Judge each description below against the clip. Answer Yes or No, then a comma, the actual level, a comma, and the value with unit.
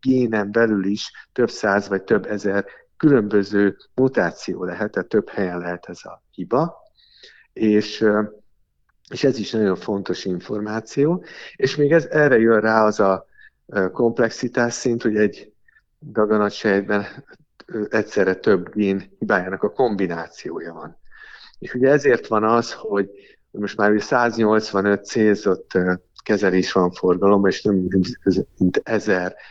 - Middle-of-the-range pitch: No, low, 105 Hz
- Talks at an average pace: Yes, average, 125 wpm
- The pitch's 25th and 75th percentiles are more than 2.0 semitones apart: Yes, average, 2.8 semitones